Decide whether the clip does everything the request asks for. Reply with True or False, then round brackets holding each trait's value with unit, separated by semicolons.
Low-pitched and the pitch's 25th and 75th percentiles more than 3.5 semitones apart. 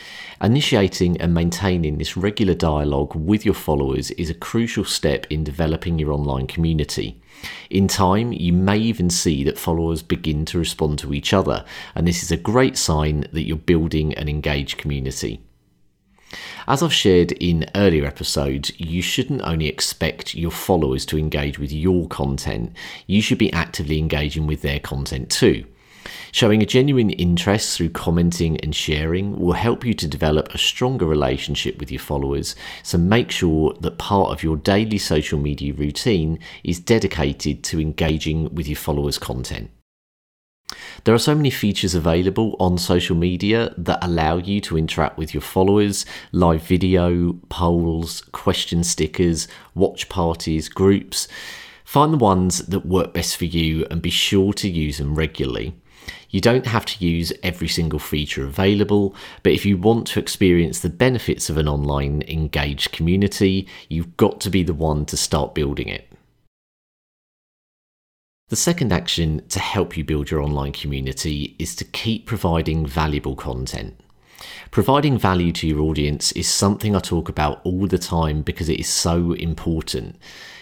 True (85 Hz; 3.9 semitones)